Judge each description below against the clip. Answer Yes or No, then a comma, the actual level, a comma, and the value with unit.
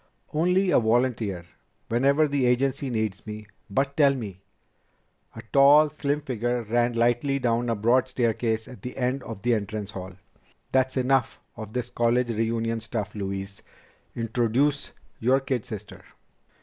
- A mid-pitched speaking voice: No, low, 120 Hz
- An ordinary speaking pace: Yes, average, 150 wpm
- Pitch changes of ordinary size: Yes, average, 3.3 semitones